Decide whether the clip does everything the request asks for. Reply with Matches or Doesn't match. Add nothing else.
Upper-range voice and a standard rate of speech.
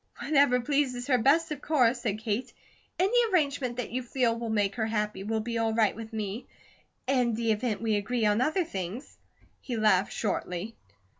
Matches